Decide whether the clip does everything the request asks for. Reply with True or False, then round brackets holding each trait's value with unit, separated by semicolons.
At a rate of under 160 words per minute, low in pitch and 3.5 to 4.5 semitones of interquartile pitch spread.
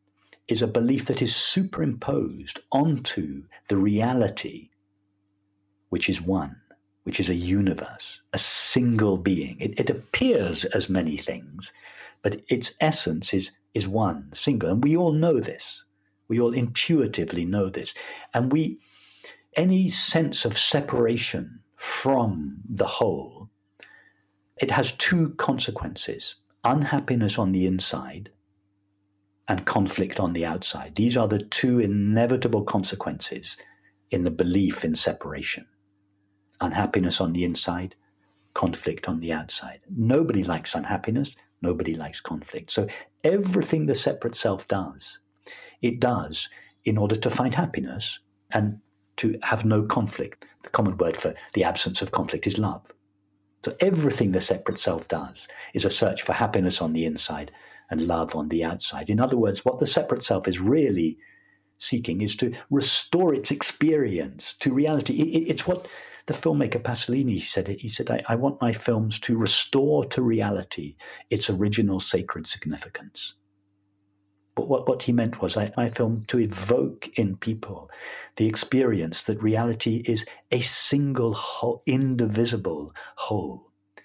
True (140 wpm; 110 Hz; 3.8 semitones)